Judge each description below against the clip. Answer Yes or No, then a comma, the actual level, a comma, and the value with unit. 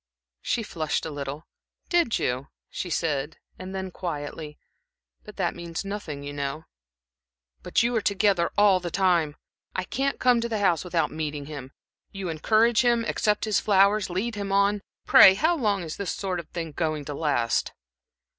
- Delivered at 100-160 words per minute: No, average, 175 wpm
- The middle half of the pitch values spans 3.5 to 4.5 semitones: No, average, 5.0 semitones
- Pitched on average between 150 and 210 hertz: Yes, medium, 185 Hz